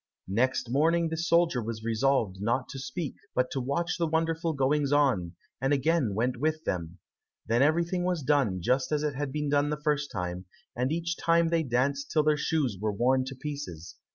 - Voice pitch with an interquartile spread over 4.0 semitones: Yes, average, 4.6 semitones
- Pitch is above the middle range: No, medium, 140 Hz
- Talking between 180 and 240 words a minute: Yes, average, 195 wpm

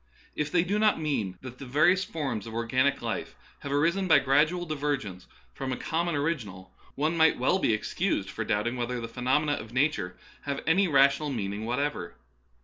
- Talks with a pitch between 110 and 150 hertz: Yes, medium, 140 Hz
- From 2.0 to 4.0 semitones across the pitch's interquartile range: No, average, 5.2 semitones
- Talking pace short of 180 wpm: No, average, 185 wpm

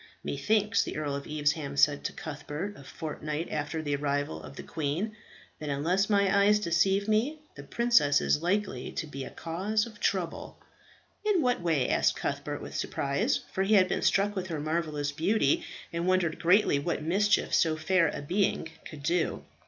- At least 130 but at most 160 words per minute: No, average, 180 wpm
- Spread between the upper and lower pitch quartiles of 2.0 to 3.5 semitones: No, wide, 5.5 semitones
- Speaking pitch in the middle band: Yes, medium, 170 Hz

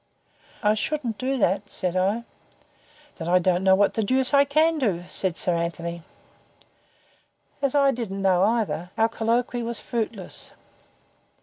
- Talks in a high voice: Yes, high, 215 Hz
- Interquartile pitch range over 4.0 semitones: Yes, average, 5.0 semitones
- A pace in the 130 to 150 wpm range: Yes, average, 145 wpm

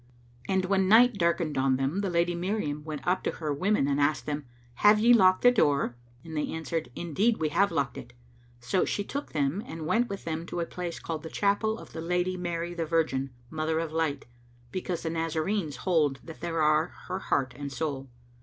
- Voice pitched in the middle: Yes, medium, 165 Hz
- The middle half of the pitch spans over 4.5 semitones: No, average, 3.7 semitones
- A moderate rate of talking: No, fast, 210 wpm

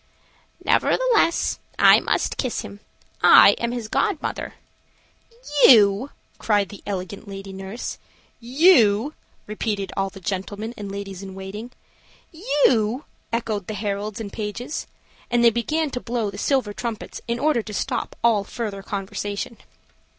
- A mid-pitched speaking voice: No, high, 215 Hz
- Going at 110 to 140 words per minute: Yes, slow, 135 wpm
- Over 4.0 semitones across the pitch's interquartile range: No, average, 3.3 semitones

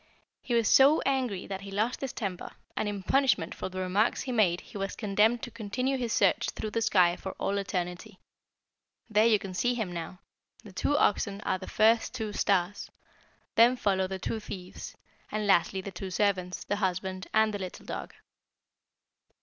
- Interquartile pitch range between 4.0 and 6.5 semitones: No, average, 3.2 semitones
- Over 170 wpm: Yes, average, 185 wpm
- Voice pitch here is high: Yes, high, 200 Hz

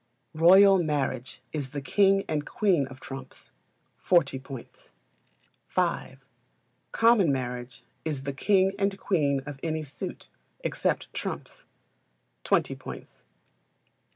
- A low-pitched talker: No, medium, 150 Hz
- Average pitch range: No, wide, 6.1 semitones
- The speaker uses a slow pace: Yes, slow, 110 wpm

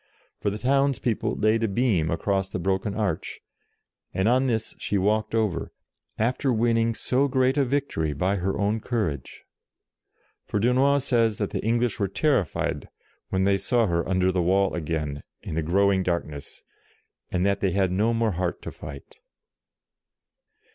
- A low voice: Yes, low, 100 Hz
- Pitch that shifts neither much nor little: Yes, average, 4.2 semitones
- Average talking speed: Yes, average, 160 wpm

